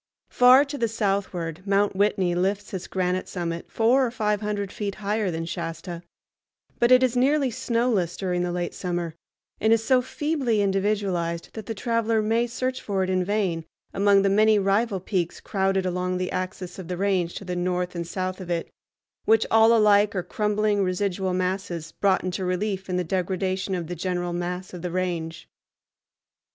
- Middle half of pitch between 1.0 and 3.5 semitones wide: Yes, average, 3.0 semitones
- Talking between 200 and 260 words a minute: No, average, 180 wpm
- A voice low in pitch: No, high, 195 Hz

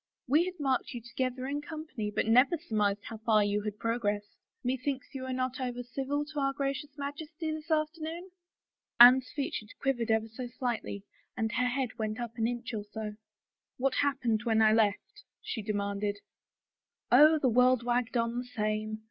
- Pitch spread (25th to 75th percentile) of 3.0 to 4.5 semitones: Yes, average, 4.0 semitones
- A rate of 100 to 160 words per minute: No, average, 190 wpm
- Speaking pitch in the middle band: No, high, 245 Hz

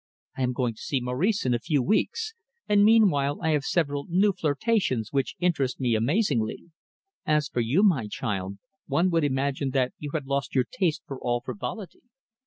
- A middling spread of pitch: No, wide, 5.8 semitones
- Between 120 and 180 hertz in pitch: Yes, medium, 140 Hz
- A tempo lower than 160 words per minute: No, average, 185 wpm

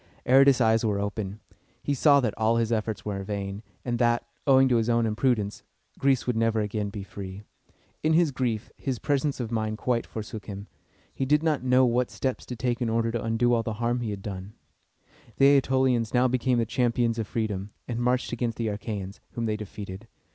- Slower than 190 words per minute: No, fast, 205 wpm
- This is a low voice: Yes, low, 115 Hz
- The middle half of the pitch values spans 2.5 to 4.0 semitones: Yes, average, 2.9 semitones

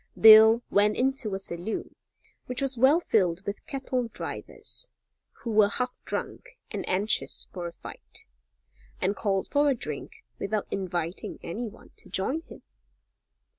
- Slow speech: No, average, 145 wpm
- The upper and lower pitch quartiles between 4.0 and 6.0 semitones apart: Yes, average, 4.6 semitones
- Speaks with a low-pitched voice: No, high, 215 Hz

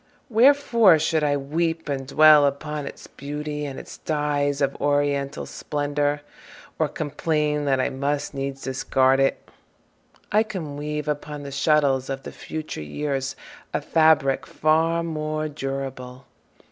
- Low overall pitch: No, medium, 145 Hz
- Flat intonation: Yes, narrow, 2.0 semitones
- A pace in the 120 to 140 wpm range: Yes, slow, 135 wpm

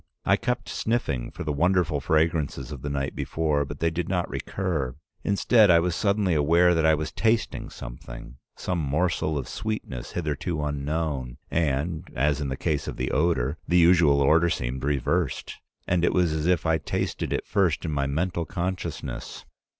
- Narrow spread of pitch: No, average, 3.8 semitones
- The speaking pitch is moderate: No, very low, 80 Hz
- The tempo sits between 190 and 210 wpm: No, average, 175 wpm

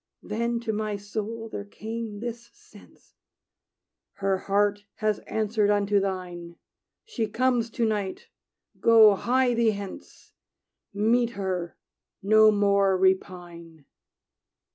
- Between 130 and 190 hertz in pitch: No, high, 210 Hz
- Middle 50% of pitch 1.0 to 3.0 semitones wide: Yes, average, 2.7 semitones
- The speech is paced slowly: Yes, slow, 110 wpm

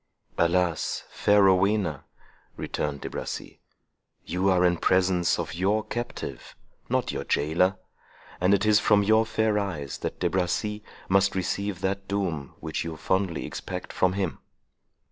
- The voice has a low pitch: Yes, very low, 95 Hz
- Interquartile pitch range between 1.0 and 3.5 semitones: Yes, narrow, 2.6 semitones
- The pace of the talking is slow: No, average, 145 wpm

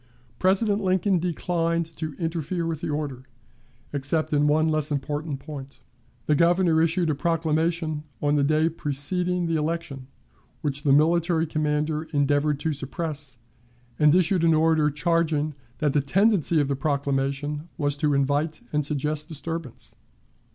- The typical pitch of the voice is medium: Yes, medium, 155 Hz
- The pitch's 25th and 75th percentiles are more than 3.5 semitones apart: No, narrow, 2.4 semitones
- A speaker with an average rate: Yes, average, 145 wpm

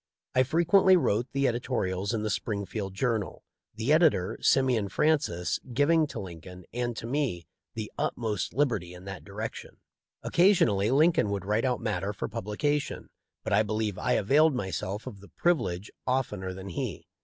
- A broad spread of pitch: Yes, wide, 5.9 semitones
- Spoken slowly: No, average, 155 wpm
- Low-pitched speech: Yes, low, 110 Hz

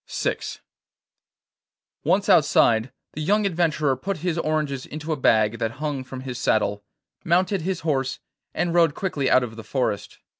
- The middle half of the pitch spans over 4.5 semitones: Yes, average, 5.0 semitones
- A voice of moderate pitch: Yes, medium, 150 Hz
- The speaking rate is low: No, average, 155 wpm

